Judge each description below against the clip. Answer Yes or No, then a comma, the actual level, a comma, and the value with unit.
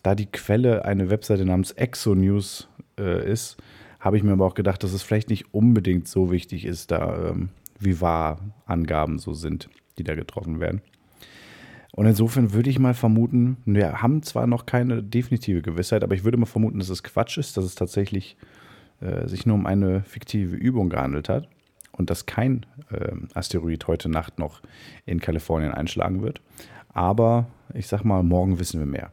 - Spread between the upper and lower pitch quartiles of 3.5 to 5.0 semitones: Yes, average, 4.3 semitones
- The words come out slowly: No, average, 180 wpm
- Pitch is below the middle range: Yes, low, 100 Hz